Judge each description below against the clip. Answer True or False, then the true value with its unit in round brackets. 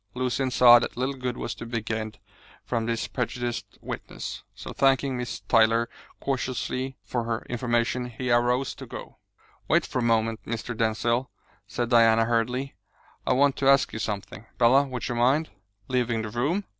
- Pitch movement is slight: True (2.0 semitones)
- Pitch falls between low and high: False (120 Hz)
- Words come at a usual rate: True (170 wpm)